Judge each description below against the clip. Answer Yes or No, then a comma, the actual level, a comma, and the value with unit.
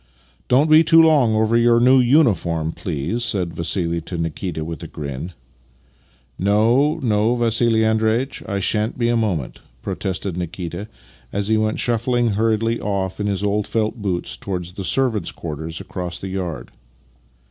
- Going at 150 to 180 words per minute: Yes, average, 165 wpm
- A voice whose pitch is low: Yes, low, 105 Hz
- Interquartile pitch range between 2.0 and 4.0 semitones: No, average, 5.0 semitones